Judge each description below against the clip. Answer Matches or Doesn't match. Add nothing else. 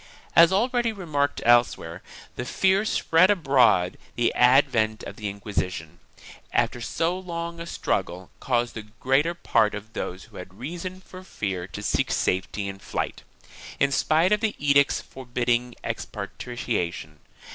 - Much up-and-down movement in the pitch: Matches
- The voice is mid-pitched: Doesn't match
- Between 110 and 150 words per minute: Matches